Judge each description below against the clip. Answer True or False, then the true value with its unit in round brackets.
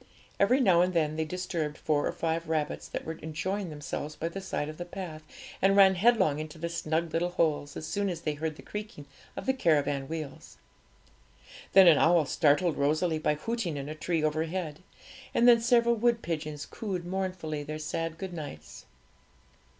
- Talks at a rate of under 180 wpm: False (185 wpm)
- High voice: False (165 Hz)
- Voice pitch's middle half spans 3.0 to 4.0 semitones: True (3.5 semitones)